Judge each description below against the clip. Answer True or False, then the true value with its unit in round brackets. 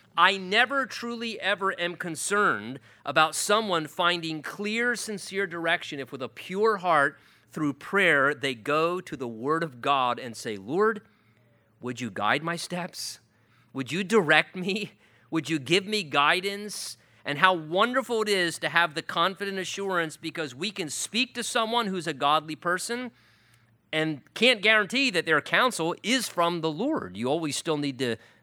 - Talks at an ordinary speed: True (165 wpm)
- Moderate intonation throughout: False (5.7 semitones)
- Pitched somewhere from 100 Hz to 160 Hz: False (170 Hz)